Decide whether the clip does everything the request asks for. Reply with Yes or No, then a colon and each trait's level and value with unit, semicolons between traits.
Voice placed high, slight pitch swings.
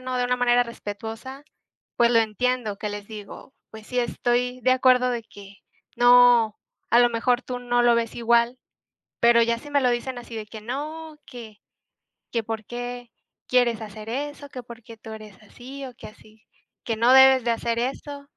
Yes: high, 240 Hz; narrow, 2.0 semitones